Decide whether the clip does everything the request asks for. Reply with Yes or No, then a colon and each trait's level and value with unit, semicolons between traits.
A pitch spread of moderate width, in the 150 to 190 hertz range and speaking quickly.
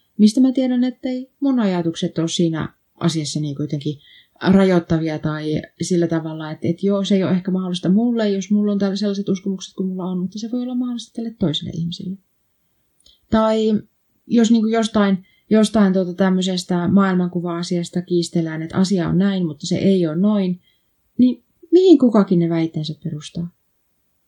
Yes: average, 3.8 semitones; medium, 185 Hz; fast, 165 wpm